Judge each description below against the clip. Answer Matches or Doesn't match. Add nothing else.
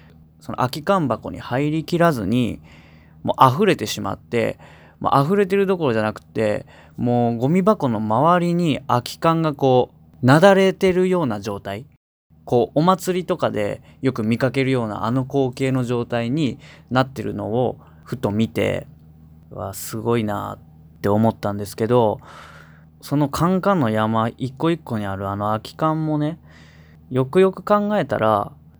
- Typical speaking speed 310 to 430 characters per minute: Doesn't match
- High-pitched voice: Doesn't match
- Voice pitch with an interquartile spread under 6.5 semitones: Doesn't match